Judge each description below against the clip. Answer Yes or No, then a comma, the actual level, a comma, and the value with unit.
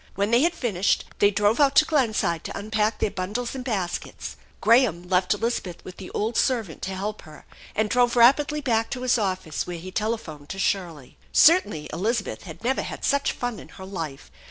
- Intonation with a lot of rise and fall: No, average, 5.0 semitones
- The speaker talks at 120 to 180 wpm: No, average, 195 wpm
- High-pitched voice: Yes, high, 210 Hz